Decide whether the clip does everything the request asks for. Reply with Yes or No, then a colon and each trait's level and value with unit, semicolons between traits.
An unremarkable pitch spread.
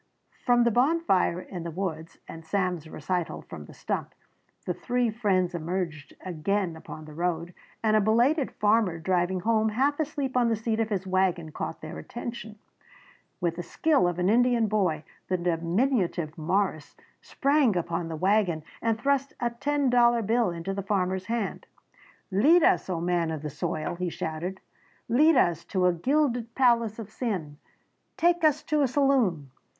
No: wide, 5.8 semitones